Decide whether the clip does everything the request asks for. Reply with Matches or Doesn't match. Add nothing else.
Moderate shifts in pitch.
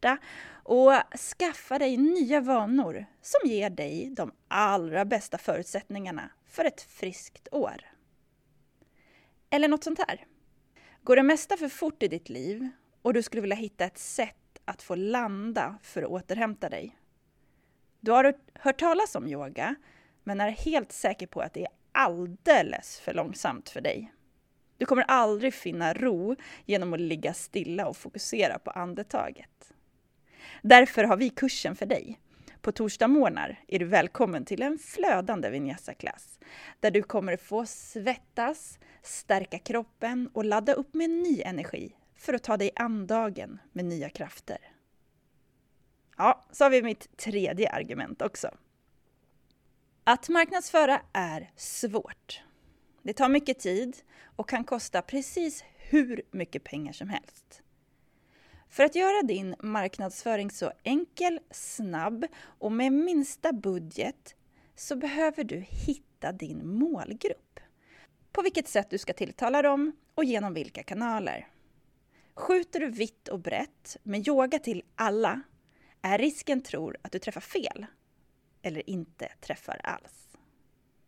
Doesn't match